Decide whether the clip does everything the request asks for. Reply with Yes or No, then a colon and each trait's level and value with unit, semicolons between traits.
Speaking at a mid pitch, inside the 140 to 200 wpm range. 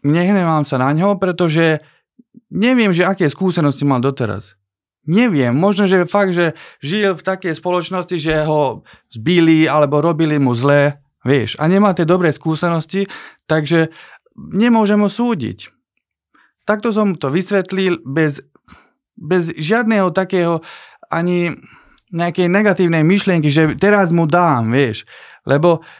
No: medium, 170 Hz; average, 125 wpm